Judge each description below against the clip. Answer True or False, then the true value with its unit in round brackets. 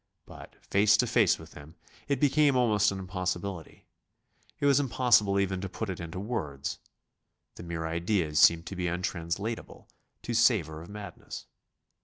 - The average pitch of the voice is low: True (95 Hz)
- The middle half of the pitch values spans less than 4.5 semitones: False (4.8 semitones)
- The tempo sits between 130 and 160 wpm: True (155 wpm)